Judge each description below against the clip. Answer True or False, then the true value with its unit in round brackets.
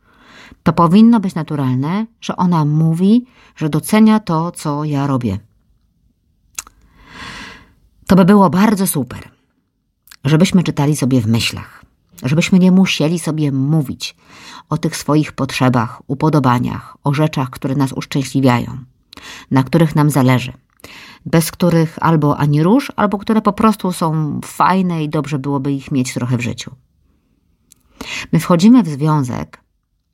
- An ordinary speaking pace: True (130 wpm)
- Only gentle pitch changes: False (5.2 semitones)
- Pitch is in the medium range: True (150 Hz)